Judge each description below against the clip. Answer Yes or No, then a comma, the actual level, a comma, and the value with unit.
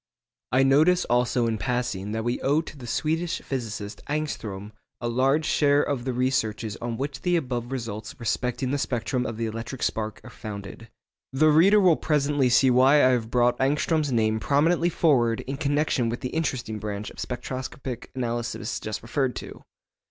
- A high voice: No, low, 125 Hz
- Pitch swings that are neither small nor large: Yes, average, 3.9 semitones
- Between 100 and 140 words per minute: No, average, 175 wpm